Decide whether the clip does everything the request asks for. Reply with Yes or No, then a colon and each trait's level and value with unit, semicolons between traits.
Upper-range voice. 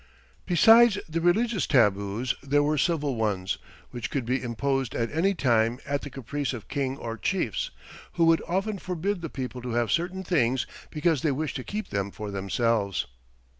No: low, 135 Hz